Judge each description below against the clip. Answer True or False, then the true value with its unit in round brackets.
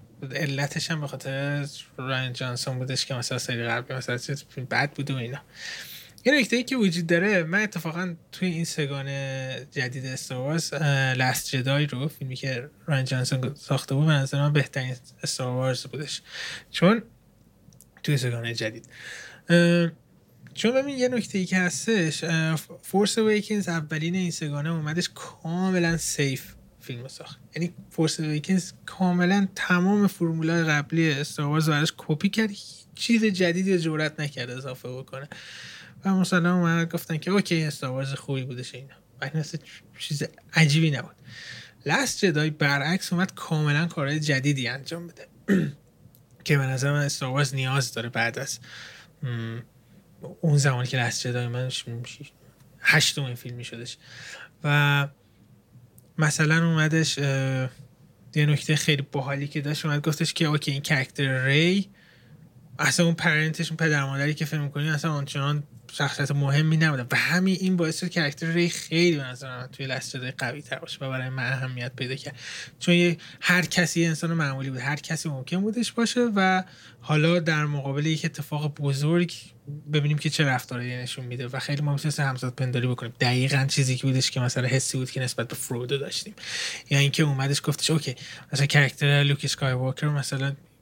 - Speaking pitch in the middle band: True (145 Hz)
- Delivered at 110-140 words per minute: False (150 wpm)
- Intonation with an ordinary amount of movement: True (3.8 semitones)